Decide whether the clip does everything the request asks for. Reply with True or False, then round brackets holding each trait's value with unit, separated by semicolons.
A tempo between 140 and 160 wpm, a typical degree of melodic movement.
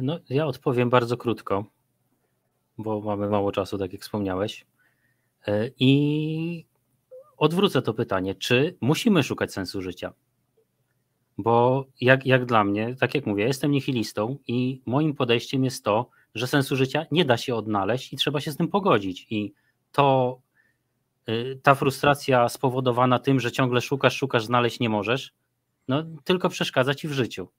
True (150 wpm; 4.1 semitones)